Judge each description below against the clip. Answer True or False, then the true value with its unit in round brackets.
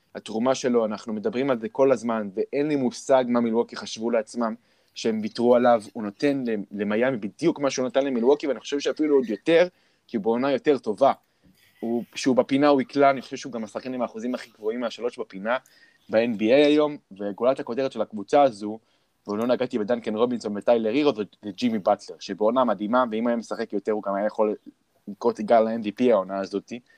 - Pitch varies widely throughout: False (3.7 semitones)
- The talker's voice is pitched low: True (120 Hz)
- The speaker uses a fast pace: True (195 wpm)